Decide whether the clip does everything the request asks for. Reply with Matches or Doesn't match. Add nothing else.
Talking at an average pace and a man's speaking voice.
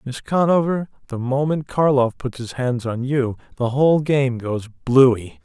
Matches